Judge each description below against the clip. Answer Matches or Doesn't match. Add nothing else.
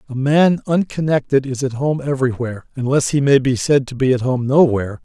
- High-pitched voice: Doesn't match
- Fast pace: Matches